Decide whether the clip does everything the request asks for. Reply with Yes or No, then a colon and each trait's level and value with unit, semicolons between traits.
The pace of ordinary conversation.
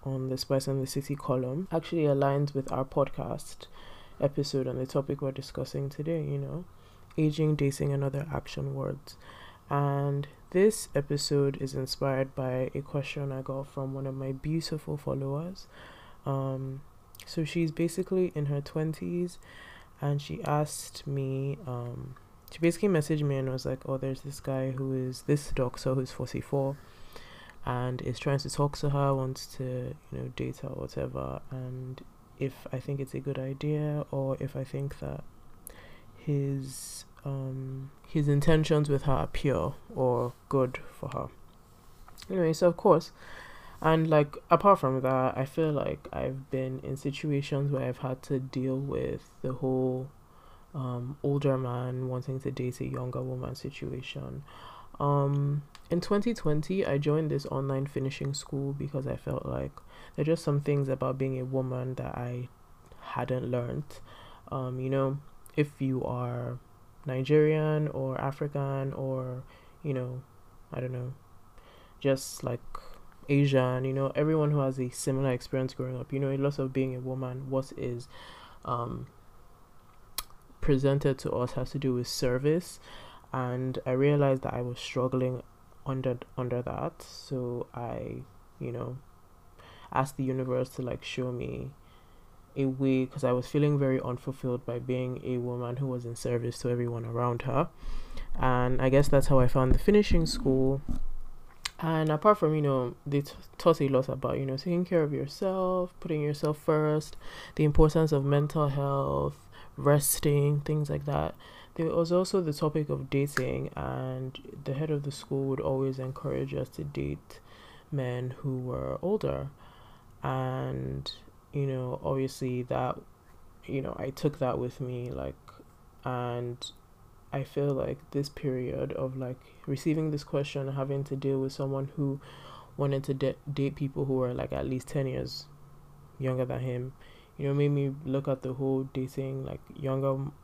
Yes: average, 160 wpm